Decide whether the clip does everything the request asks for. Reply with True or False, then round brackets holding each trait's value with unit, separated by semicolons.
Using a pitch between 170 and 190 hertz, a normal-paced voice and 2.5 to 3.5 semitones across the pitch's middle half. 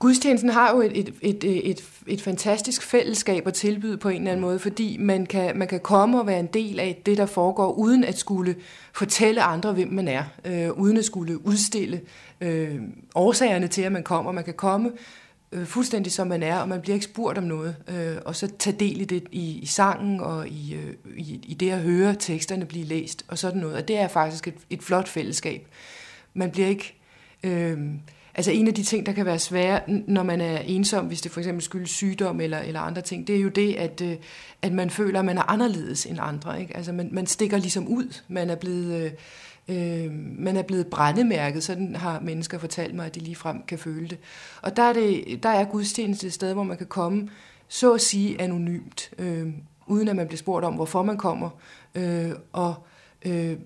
True (185 Hz; 215 wpm; 3.0 semitones)